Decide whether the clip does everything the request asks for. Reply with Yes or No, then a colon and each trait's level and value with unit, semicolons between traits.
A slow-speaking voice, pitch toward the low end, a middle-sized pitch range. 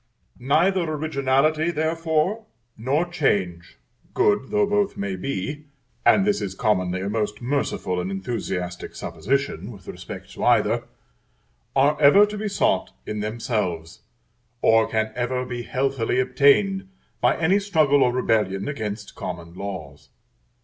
No: slow, 130 wpm; low, 125 Hz; wide, 7.4 semitones